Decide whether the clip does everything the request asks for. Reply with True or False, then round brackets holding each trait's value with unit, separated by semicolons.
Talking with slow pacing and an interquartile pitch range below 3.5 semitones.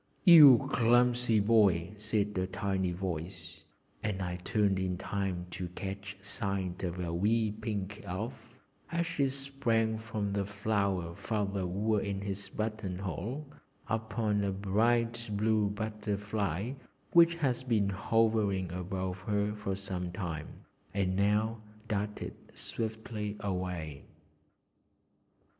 True (120 wpm; 2.9 semitones)